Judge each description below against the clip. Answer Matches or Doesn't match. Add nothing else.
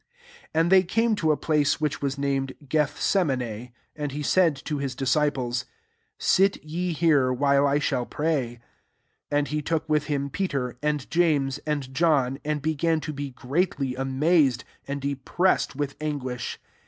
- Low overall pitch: Doesn't match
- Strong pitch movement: Doesn't match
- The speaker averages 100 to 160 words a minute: Matches